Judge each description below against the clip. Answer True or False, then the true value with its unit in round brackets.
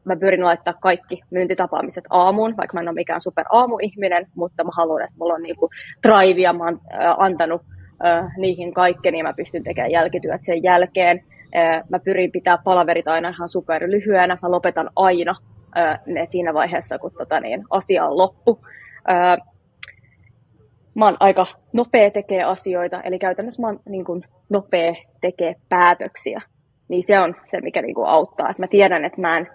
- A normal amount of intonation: False (1.8 semitones)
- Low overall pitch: False (180 Hz)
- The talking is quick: True (175 wpm)